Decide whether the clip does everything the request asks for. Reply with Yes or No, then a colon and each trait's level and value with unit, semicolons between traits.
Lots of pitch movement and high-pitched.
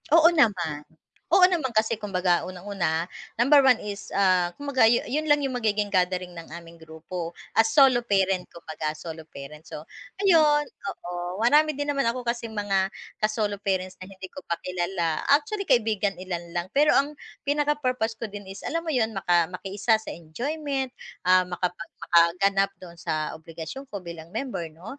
Yes: wide, 6.5 semitones; high, 200 Hz